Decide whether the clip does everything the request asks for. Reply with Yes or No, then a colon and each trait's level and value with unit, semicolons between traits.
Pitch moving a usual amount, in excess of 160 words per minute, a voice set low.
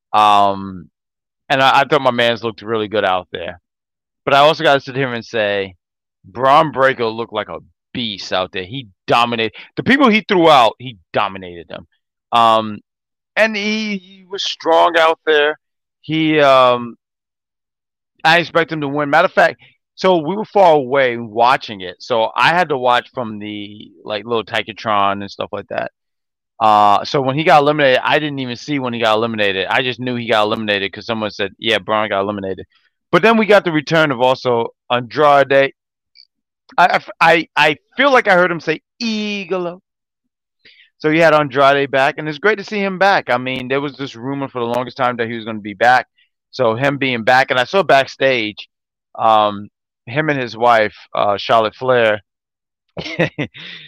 No: wide, 6.2 semitones; average, 185 wpm; low, 130 Hz